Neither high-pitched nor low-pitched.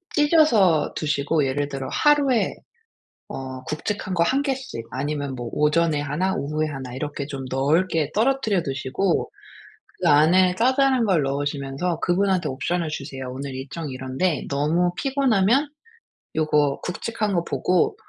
Yes: medium, 155 Hz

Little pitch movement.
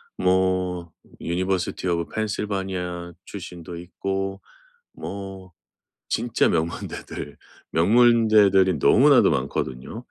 Yes: narrow, 2.2 semitones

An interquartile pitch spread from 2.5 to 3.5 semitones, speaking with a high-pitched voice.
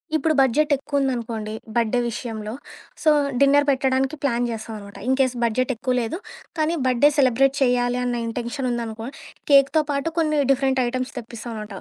Yes: average, 2.9 semitones; very high, 255 Hz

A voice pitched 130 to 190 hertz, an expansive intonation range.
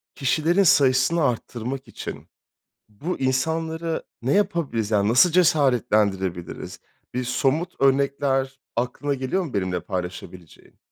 Yes: low, 135 Hz; wide, 6.0 semitones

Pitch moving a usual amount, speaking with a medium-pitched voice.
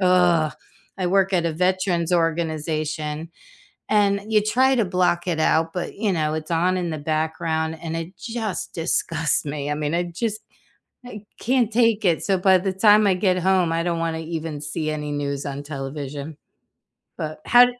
Yes: average, 3.6 semitones; medium, 170 Hz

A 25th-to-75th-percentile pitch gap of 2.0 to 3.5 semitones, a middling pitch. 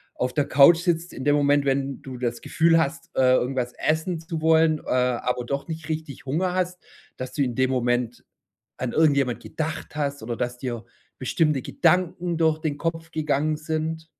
No: average, 4.0 semitones; medium, 145 Hz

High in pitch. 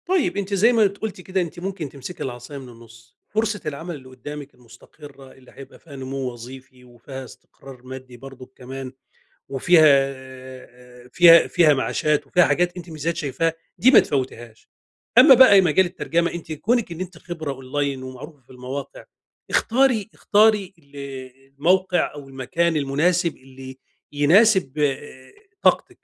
No: medium, 145 Hz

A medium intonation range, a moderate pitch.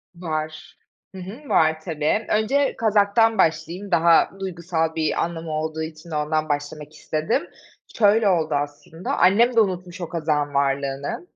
Yes: average, 4.4 semitones; medium, 165 Hz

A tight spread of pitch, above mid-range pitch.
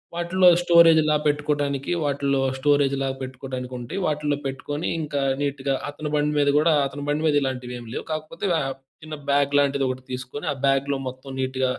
No: narrow, 2.0 semitones; medium, 140 Hz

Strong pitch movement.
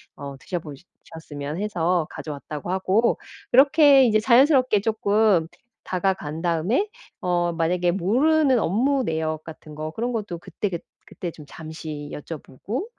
Yes: wide, 6.3 semitones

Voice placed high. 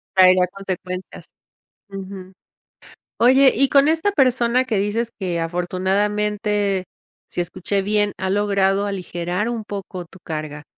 Yes: high, 195 Hz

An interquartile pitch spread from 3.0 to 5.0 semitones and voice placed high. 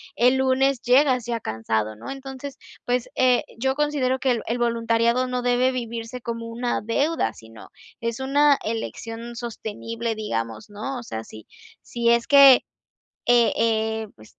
No: narrow, 2.4 semitones; high, 235 Hz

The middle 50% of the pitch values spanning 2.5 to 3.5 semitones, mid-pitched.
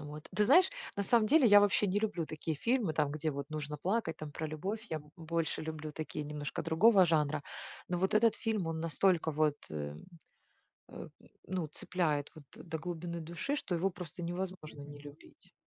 No: average, 3.9 semitones; medium, 165 Hz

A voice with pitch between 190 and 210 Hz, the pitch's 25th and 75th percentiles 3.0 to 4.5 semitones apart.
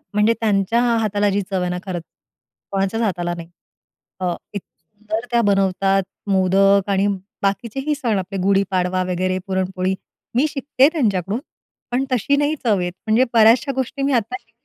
Yes: high, 200 Hz; average, 3.7 semitones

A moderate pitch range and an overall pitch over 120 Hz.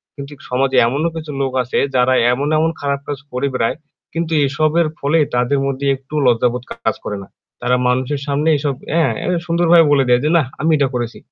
Yes: average, 3.4 semitones; medium, 140 Hz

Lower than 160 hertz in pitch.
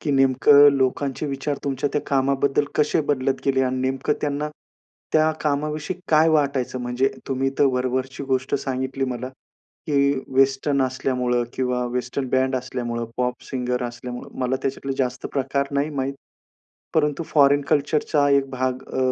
Yes: low, 135 Hz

